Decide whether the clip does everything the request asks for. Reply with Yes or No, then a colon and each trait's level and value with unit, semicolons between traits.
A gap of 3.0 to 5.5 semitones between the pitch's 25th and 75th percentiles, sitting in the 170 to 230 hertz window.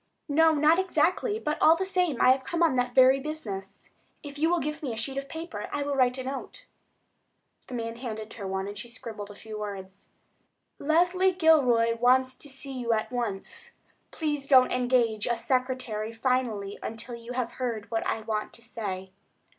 No: average, 4.7 semitones; very high, 255 Hz